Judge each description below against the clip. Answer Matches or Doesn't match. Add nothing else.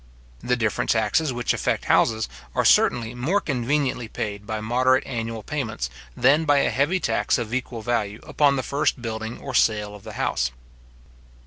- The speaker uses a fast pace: Doesn't match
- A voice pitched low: Matches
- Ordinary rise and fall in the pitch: Matches